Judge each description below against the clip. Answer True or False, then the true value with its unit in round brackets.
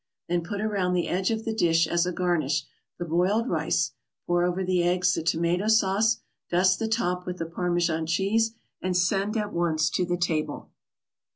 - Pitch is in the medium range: True (180 Hz)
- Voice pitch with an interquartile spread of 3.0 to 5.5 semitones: False (2.5 semitones)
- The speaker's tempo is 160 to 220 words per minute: True (185 wpm)